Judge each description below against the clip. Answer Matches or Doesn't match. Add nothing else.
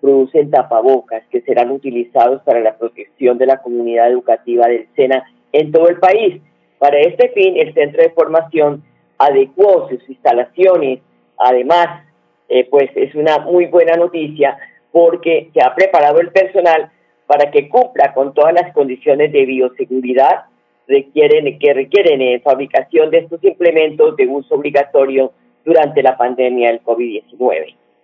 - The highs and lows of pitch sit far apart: Matches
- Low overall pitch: Doesn't match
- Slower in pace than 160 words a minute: Matches